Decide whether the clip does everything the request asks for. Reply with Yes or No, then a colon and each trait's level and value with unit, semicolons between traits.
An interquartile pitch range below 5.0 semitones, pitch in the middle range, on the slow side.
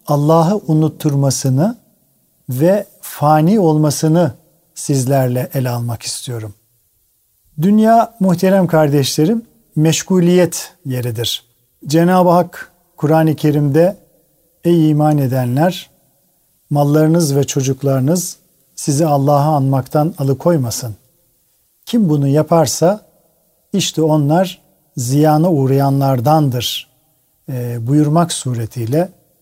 Yes: average, 4.0 semitones; medium, 155 Hz; slow, 75 wpm